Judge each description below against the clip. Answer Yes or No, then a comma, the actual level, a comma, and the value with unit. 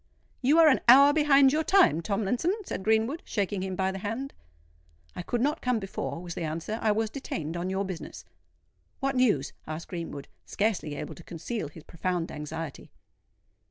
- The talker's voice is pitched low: No, high, 205 Hz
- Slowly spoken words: No, average, 175 wpm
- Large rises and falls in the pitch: Yes, wide, 7.5 semitones